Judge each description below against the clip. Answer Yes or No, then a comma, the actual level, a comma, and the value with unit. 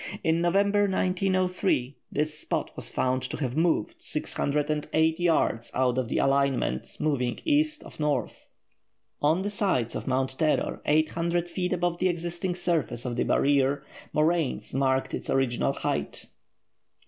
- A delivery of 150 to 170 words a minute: No, average, 140 wpm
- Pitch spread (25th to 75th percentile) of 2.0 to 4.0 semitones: No, average, 4.8 semitones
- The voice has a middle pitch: Yes, medium, 155 Hz